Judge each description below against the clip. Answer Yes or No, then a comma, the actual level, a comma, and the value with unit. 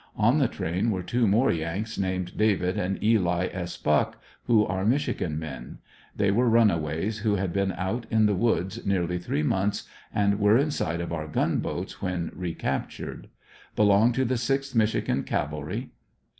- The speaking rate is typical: Yes, average, 165 wpm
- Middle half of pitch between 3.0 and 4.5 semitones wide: Yes, average, 4.1 semitones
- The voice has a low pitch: Yes, low, 100 Hz